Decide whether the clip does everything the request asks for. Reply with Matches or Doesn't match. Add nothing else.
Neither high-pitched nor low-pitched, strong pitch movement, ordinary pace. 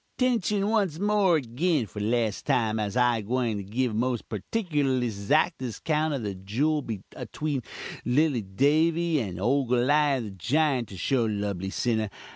Doesn't match